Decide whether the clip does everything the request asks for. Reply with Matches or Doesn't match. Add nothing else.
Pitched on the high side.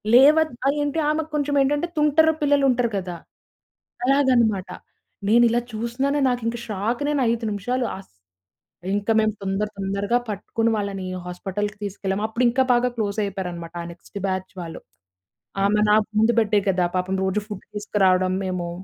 Matches